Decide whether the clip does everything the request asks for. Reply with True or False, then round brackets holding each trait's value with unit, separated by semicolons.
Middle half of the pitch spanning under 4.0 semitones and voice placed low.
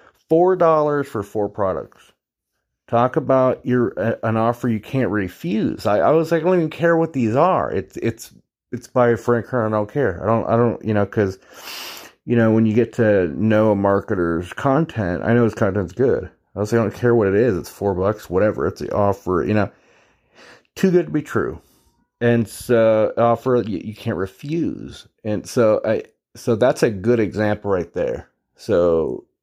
False (4.4 semitones; 115 Hz)